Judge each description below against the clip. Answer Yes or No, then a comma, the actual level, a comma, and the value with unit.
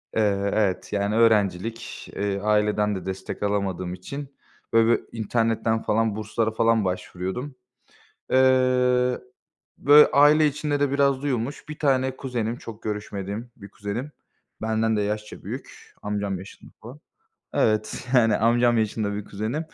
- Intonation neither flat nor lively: Yes, average, 3.6 semitones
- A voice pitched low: Yes, low, 110 Hz